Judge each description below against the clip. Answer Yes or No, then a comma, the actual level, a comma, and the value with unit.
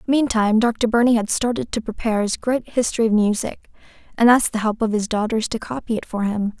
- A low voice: No, high, 225 Hz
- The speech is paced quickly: Yes, fast, 220 wpm